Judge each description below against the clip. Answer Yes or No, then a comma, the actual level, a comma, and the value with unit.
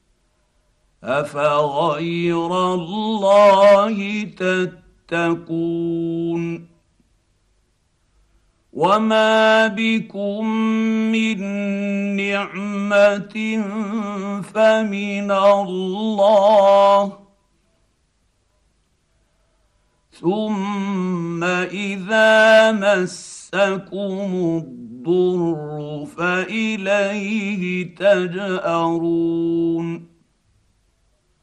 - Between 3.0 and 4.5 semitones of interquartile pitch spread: Yes, average, 3.4 semitones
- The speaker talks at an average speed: No, slow, 30 wpm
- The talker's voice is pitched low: No, high, 200 Hz